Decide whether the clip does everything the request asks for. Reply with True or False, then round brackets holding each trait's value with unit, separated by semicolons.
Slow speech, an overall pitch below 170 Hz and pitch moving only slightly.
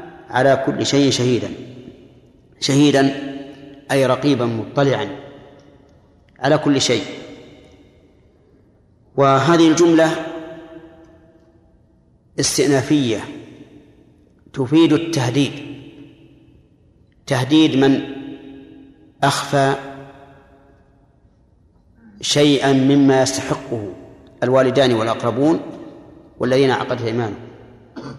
True (55 wpm; 140 Hz; 1.9 semitones)